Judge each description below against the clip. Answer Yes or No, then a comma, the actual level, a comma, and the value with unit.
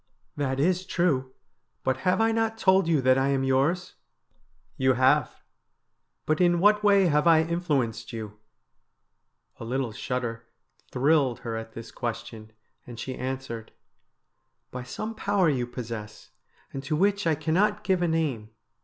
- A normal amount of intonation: No, wide, 6.2 semitones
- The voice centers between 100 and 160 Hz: Yes, low, 135 Hz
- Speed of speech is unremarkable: Yes, average, 165 wpm